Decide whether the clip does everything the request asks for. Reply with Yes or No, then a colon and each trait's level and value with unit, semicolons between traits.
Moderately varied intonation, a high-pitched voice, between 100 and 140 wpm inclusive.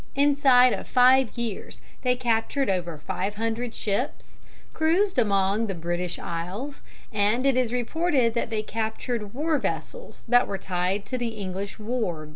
No: average, 4.3 semitones; high, 230 Hz; average, 150 wpm